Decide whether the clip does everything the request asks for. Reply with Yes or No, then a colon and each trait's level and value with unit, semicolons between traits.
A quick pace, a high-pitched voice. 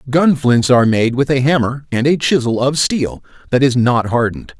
No: fast, 210 wpm; low, 130 Hz